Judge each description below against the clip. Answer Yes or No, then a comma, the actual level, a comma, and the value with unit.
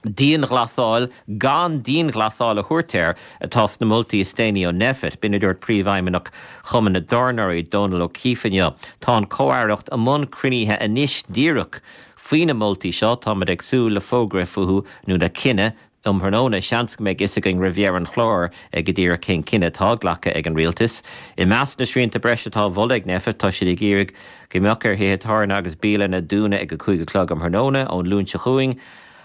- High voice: No, low, 105 Hz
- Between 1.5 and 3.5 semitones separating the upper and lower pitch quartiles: No, average, 4.2 semitones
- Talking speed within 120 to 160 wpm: Yes, average, 145 wpm